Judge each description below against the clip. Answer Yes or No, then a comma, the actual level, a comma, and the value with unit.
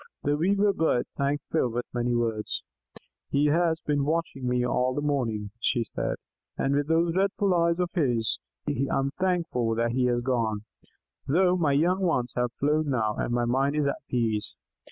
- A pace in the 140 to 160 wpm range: No, average, 175 wpm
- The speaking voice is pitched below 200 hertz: Yes, medium, 140 Hz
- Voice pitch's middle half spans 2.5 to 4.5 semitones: No, average, 5.3 semitones